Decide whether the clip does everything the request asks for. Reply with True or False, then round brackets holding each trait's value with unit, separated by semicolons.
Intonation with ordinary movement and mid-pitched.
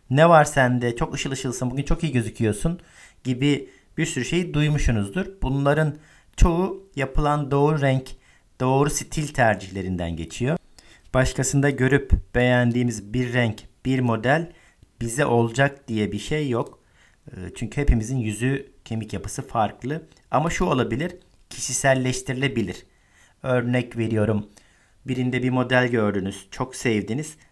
False (4.1 semitones; 130 Hz)